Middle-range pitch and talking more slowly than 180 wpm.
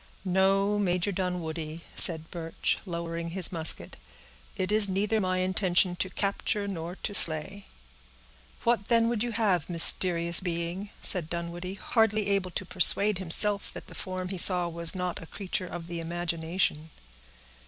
Yes: medium, 180 Hz; average, 150 wpm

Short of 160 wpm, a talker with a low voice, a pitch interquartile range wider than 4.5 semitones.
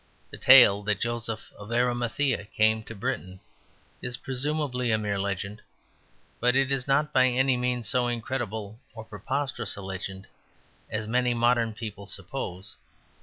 No: average, 145 wpm; low, 120 Hz; average, 3.3 semitones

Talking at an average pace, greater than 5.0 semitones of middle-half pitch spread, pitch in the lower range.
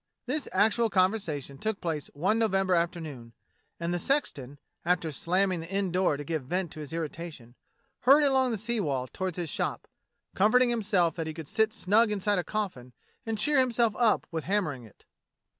No: average, 185 wpm; wide, 5.5 semitones; medium, 185 Hz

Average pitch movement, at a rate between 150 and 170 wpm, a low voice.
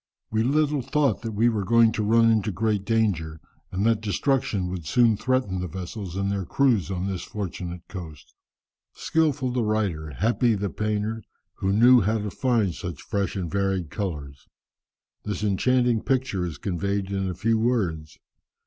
Yes: average, 3.8 semitones; average, 165 wpm; low, 105 Hz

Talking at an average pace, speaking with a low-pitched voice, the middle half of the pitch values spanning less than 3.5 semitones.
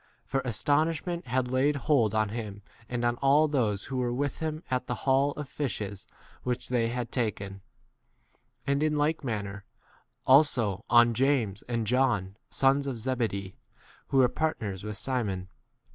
No: average, 160 wpm; low, 125 Hz; average, 4.4 semitones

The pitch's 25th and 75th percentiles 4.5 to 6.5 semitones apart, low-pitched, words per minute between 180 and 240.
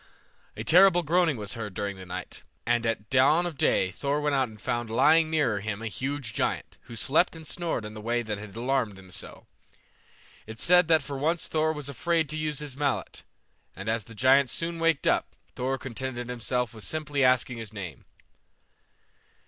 Yes: wide, 5.5 semitones; low, 130 Hz; average, 195 wpm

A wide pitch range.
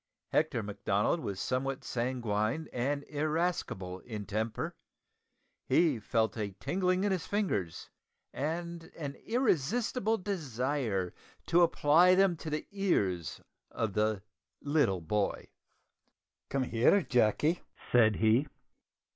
Yes: wide, 8.0 semitones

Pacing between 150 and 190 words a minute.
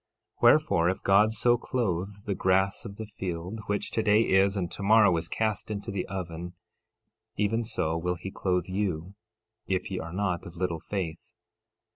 Yes: average, 170 wpm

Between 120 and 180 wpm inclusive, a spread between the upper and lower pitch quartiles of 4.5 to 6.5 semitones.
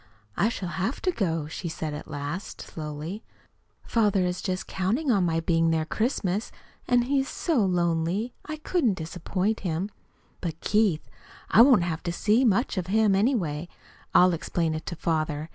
Yes: average, 170 wpm; average, 5.1 semitones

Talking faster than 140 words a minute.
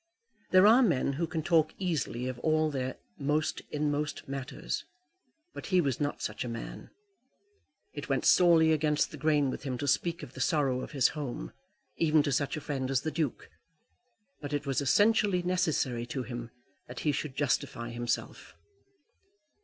Yes: average, 170 wpm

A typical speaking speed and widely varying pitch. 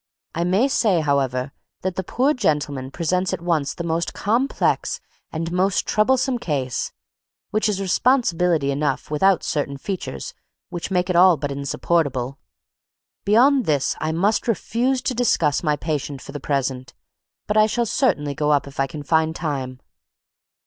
Yes: average, 155 wpm; wide, 6.2 semitones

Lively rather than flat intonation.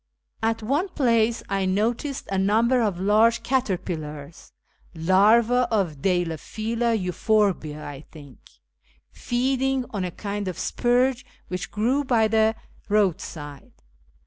No: average, 4.6 semitones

